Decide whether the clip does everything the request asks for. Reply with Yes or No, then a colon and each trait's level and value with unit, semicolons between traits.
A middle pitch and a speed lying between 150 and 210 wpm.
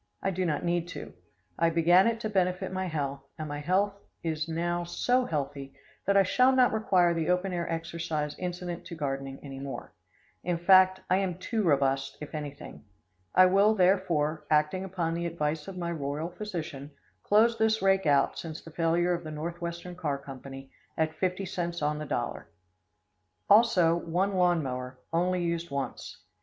Yes: medium, 170 Hz; average, 175 wpm